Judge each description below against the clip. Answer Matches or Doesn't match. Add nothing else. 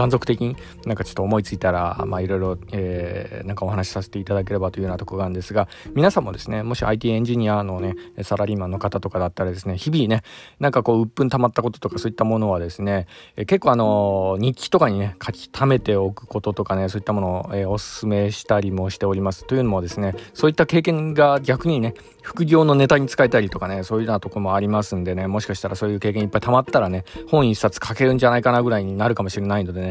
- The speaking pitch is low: Matches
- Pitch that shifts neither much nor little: Matches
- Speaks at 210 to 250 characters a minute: Doesn't match